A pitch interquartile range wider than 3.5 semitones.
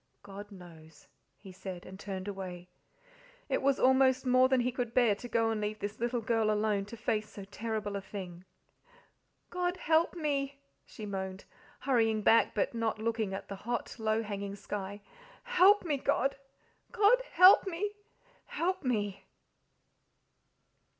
Yes: average, 4.6 semitones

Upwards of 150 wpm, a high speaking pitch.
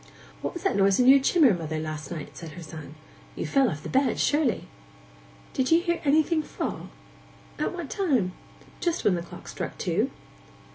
Yes: average, 185 wpm; very high, 255 Hz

